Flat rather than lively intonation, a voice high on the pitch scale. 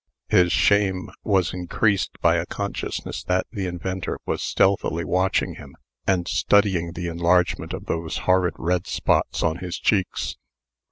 No: narrow, 1.7 semitones; very low, 90 Hz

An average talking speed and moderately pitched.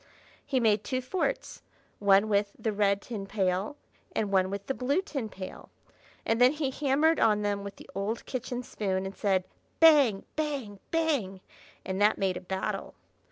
No: average, 170 wpm; high, 210 Hz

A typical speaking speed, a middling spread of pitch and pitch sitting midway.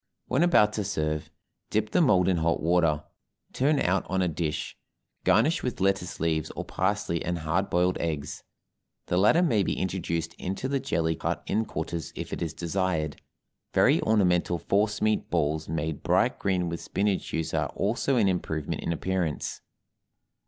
No: average, 165 wpm; average, 4.3 semitones; very low, 90 Hz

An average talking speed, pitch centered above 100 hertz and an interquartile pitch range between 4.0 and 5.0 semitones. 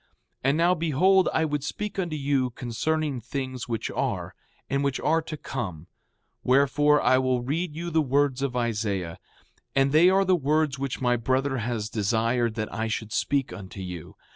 Yes: average, 180 wpm; low, 135 Hz; average, 4.5 semitones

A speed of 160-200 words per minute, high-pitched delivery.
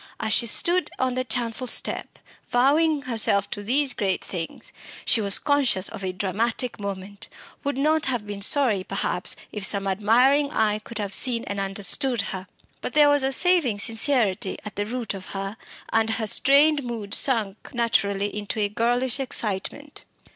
Yes: average, 170 wpm; high, 225 Hz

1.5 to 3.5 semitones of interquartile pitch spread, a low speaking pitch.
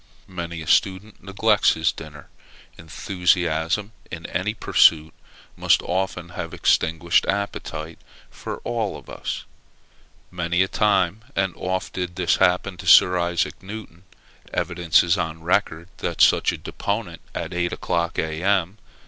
Yes: narrow, 2.5 semitones; very low, 90 Hz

